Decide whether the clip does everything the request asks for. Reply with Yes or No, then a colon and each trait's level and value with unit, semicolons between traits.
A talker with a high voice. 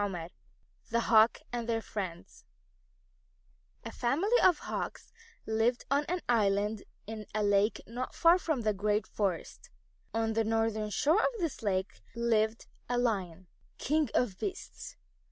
Yes: high, 225 Hz